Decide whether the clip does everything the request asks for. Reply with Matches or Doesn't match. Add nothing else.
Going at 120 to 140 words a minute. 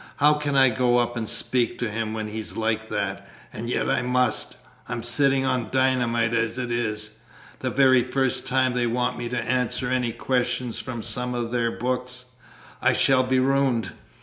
Doesn't match